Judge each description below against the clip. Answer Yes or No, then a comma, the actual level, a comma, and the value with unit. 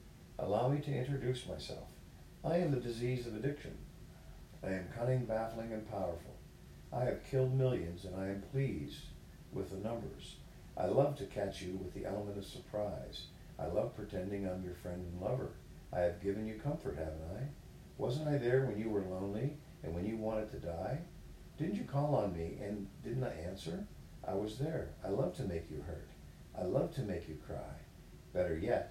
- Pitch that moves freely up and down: Yes, wide, 5.7 semitones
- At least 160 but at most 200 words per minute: Yes, average, 190 wpm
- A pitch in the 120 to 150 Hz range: No, low, 105 Hz